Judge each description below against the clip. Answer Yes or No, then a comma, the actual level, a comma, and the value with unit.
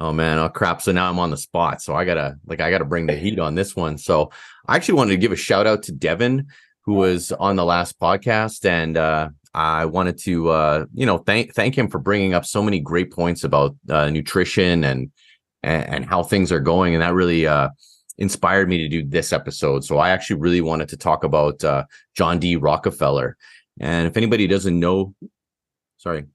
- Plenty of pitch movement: No, average, 3.6 semitones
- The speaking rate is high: Yes, fast, 215 wpm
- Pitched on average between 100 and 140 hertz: No, very low, 85 Hz